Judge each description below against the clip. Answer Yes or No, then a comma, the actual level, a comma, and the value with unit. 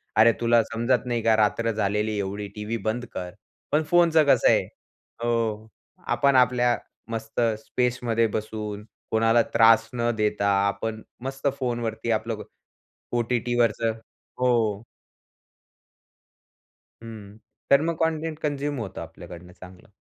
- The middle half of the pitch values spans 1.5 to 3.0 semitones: Yes, narrow, 2.4 semitones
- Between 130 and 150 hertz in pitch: No, low, 115 Hz